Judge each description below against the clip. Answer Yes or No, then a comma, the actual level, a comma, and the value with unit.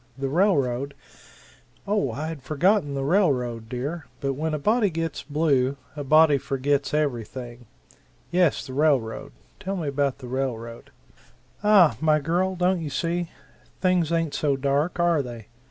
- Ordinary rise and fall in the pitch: Yes, average, 4.1 semitones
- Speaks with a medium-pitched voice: Yes, medium, 145 Hz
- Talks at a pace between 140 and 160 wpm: Yes, average, 155 wpm